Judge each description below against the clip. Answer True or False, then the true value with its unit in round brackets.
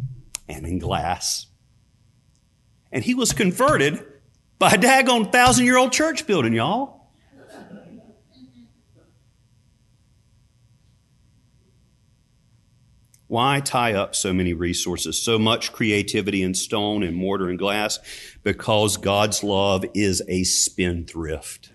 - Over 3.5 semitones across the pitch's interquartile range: True (4.7 semitones)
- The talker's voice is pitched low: True (115 Hz)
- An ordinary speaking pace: False (100 wpm)